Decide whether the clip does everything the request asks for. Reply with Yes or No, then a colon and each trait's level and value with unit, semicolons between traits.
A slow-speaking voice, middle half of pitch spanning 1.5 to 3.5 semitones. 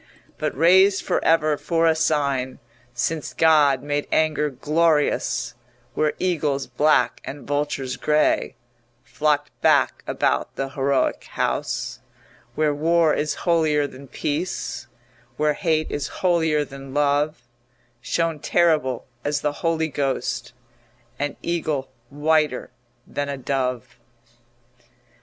Yes: slow, 115 wpm; narrow, 2.4 semitones